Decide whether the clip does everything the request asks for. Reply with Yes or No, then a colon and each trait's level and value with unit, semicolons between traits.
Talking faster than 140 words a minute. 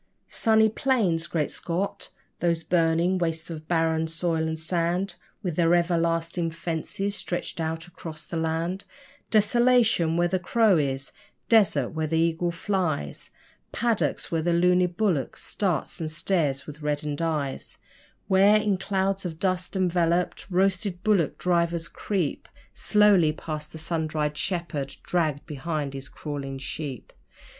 No: slow, 135 wpm